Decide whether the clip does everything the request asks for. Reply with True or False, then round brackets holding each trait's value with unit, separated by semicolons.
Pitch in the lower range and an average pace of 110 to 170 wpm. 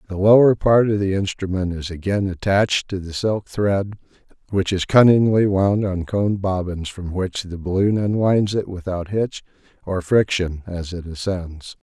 True (95 Hz; 165 wpm)